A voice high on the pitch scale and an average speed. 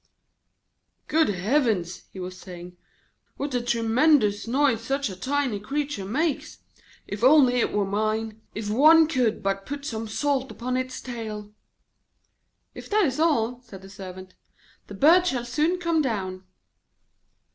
Yes: high, 235 Hz; average, 145 wpm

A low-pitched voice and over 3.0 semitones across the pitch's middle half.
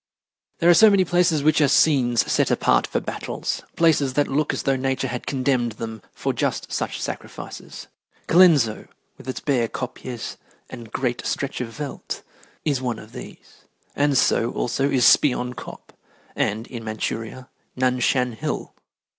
Yes: low, 130 Hz; average, 3.4 semitones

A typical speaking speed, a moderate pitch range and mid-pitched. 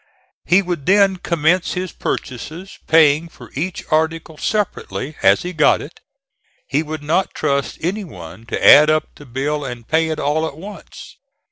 Yes: average, 165 wpm; average, 3.4 semitones; medium, 160 Hz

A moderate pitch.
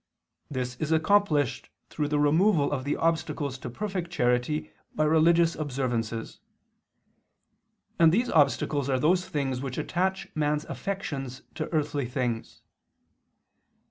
Yes: medium, 150 Hz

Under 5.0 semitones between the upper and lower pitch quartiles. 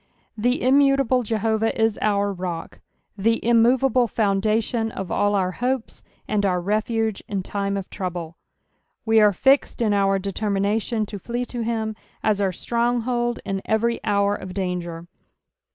Yes: average, 3.1 semitones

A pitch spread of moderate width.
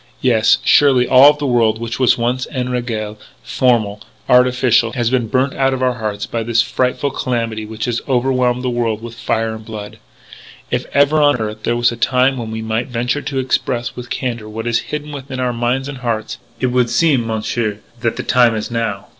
No: narrow, 2.3 semitones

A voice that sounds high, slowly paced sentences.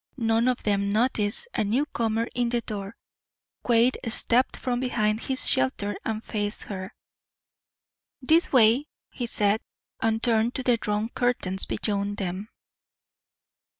Yes: high, 225 Hz; slow, 130 wpm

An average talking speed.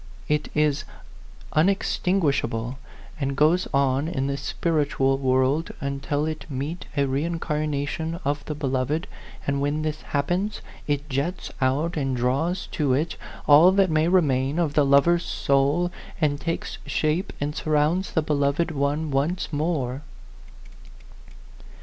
No: slow, 130 wpm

